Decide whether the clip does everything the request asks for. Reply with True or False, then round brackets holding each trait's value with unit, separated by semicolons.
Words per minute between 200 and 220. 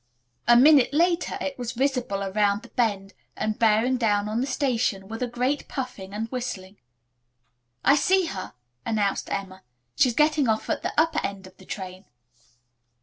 False (165 wpm)